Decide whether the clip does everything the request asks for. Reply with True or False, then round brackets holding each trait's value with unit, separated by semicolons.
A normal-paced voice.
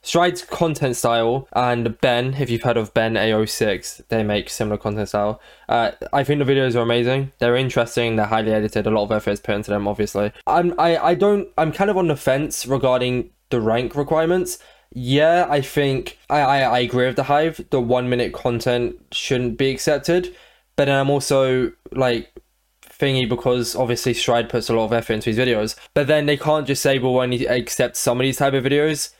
False (210 wpm)